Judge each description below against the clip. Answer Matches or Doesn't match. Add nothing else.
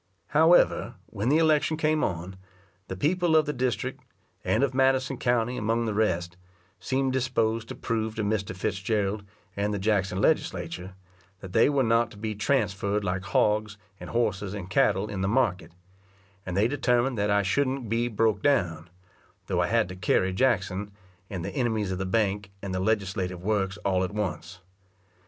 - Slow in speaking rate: Doesn't match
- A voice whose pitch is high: Doesn't match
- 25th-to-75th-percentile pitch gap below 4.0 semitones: Doesn't match